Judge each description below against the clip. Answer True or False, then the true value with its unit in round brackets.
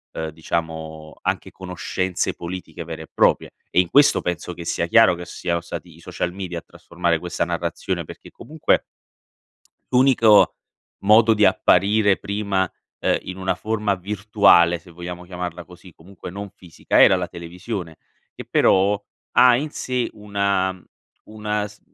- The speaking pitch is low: True (90 Hz)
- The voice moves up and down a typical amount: True (3.3 semitones)